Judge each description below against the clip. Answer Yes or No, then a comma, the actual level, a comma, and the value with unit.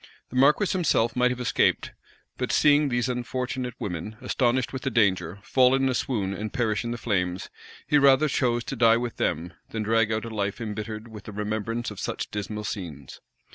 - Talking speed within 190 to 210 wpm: Yes, average, 195 wpm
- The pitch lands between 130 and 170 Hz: No, low, 115 Hz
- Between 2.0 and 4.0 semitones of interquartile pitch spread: Yes, average, 3.3 semitones